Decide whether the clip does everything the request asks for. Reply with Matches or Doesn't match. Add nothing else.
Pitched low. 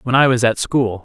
Matches